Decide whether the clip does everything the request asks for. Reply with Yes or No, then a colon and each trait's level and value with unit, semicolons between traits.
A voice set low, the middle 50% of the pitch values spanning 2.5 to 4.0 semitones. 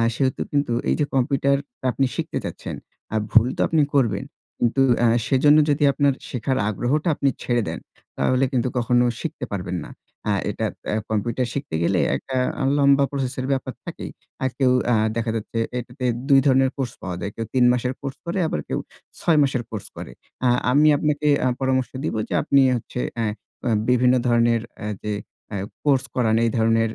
Yes: low, 130 Hz; average, 3.0 semitones